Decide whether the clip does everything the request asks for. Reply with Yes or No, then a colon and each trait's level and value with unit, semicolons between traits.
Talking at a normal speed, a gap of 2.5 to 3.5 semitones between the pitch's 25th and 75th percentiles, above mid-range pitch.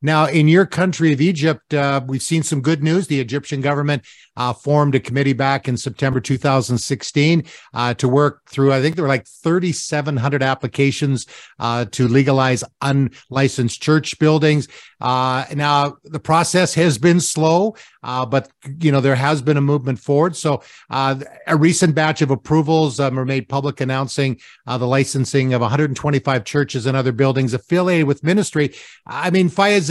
No: average, 170 wpm; average, 2.8 semitones; medium, 140 Hz